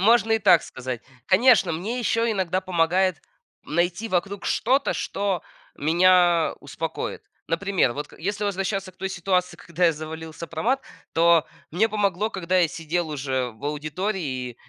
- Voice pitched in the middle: Yes, medium, 180 Hz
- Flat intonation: No, average, 3.8 semitones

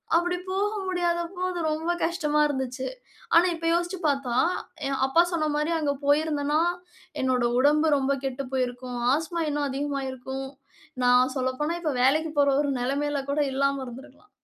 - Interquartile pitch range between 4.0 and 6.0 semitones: No, average, 3.4 semitones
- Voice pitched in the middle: No, very high, 285 Hz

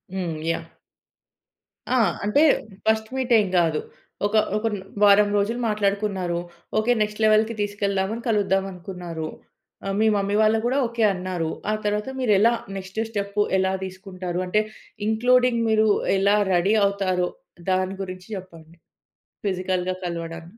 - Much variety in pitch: No, average, 2.8 semitones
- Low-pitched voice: No, high, 200 Hz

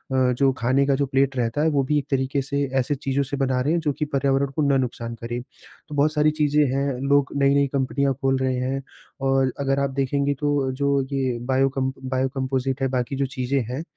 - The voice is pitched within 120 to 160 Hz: Yes, low, 135 Hz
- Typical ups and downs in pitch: No, narrow, 1.3 semitones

